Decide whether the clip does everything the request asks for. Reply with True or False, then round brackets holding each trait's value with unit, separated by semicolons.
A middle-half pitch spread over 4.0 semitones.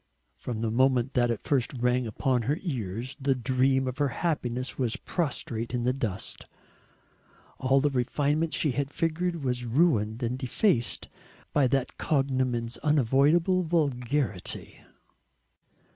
False (3.2 semitones)